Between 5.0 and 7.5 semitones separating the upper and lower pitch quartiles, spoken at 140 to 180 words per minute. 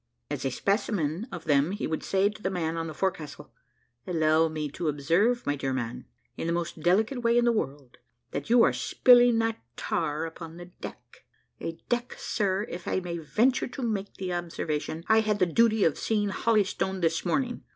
No: wide, 5.6 semitones; average, 195 wpm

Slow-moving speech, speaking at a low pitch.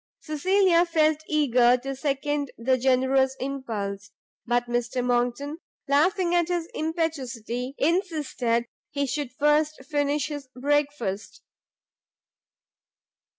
No: slow, 100 wpm; very high, 280 Hz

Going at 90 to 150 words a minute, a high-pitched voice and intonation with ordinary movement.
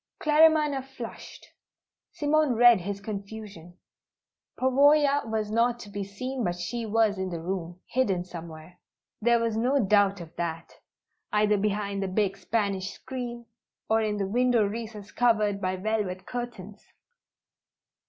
Yes: slow, 135 wpm; high, 210 Hz; average, 3.8 semitones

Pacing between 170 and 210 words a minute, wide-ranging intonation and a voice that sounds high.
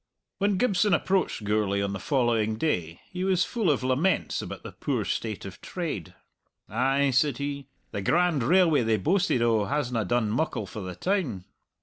No: average, 175 wpm; wide, 8.5 semitones; low, 135 Hz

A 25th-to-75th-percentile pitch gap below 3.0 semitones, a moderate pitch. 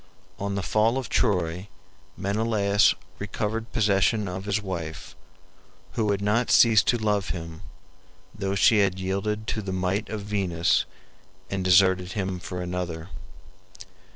No: narrow, 2.5 semitones; low, 100 Hz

